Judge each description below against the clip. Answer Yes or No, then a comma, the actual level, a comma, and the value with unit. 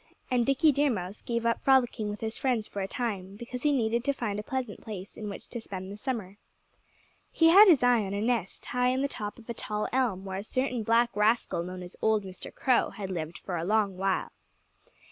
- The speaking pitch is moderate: No, high, 220 Hz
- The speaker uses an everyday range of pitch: Yes, average, 4.0 semitones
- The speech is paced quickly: Yes, fast, 230 wpm